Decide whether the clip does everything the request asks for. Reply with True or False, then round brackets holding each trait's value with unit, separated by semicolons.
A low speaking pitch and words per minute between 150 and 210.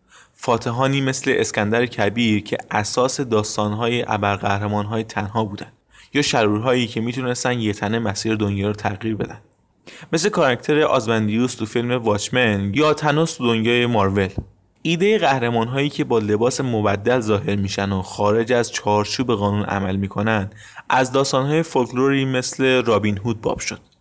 False (115 Hz; 135 wpm)